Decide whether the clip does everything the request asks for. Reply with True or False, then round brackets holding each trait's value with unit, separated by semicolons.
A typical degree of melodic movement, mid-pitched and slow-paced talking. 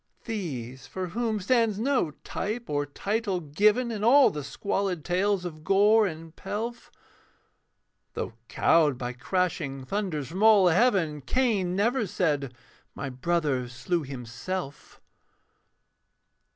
False (6.4 semitones; 180 Hz; 120 wpm)